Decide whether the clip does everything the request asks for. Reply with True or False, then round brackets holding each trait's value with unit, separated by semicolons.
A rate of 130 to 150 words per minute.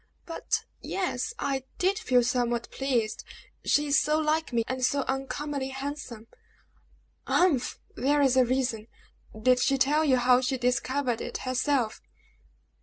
True (145 wpm)